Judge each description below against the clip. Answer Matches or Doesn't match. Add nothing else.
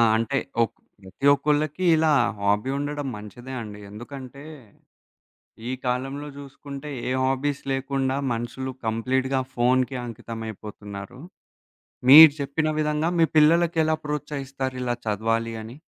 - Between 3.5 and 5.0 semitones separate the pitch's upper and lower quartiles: Matches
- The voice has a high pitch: Doesn't match